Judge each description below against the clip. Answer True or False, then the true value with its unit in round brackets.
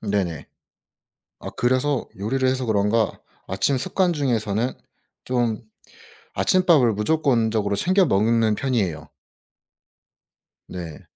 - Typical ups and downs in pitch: True (4.5 semitones)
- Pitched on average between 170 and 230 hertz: False (115 Hz)